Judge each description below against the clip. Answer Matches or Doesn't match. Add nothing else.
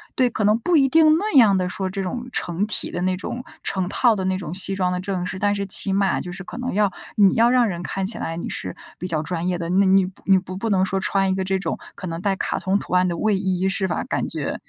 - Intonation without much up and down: Matches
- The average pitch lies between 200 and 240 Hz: Doesn't match